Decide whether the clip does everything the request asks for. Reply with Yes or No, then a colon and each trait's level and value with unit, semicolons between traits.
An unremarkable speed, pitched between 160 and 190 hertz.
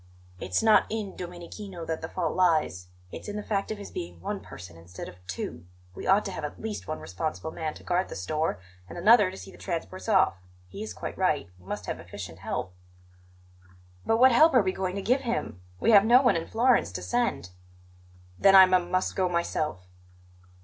No: fast, 210 wpm; medium, 185 Hz